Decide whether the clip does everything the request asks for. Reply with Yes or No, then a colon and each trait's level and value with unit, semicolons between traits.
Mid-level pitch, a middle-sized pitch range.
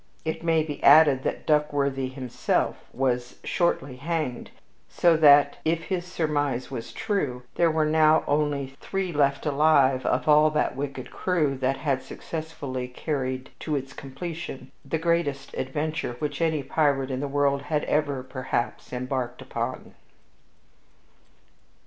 Yes: medium, 145 Hz; average, 3.1 semitones